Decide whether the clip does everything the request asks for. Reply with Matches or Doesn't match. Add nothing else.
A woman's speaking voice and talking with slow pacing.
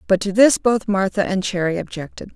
Doesn't match